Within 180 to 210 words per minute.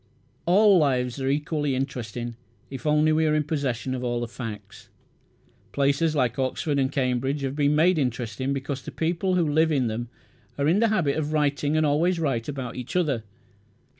Yes: average, 185 wpm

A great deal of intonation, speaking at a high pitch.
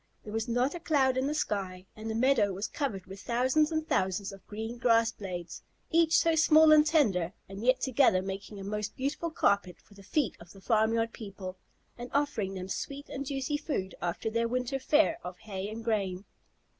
Yes: wide, 6.0 semitones; high, 225 Hz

